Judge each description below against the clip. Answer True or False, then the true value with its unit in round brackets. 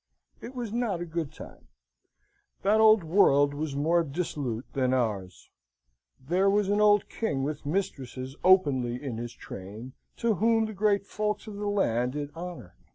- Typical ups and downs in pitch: False (7.8 semitones)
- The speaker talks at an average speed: True (160 wpm)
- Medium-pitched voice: True (165 Hz)